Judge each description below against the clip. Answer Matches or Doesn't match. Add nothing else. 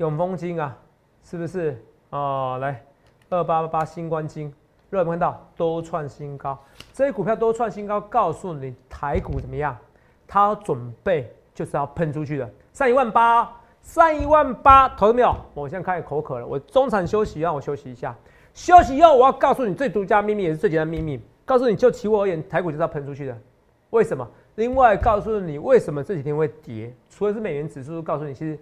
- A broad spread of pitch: Matches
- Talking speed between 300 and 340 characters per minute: Matches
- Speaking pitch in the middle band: Matches